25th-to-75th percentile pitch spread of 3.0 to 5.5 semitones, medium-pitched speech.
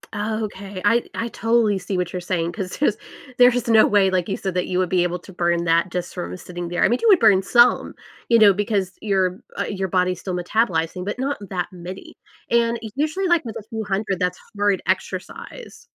No: average, 3.9 semitones; high, 195 Hz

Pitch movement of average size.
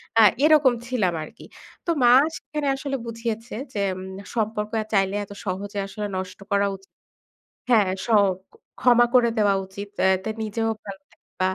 Yes: average, 3.4 semitones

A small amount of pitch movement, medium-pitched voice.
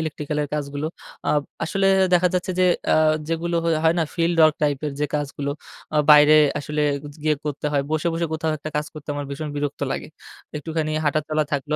Yes: narrow, 1.7 semitones; medium, 150 Hz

